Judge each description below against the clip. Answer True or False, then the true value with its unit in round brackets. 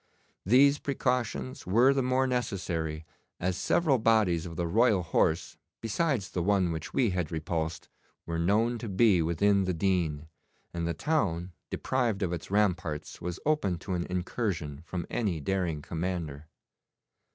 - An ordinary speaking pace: True (150 wpm)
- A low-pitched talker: True (95 Hz)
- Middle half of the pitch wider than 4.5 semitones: True (5.4 semitones)